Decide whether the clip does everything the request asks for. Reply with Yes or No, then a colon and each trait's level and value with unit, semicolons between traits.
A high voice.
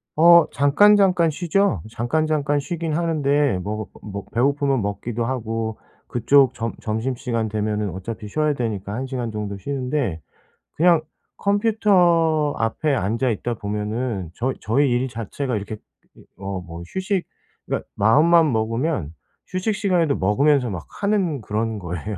No: low, 125 Hz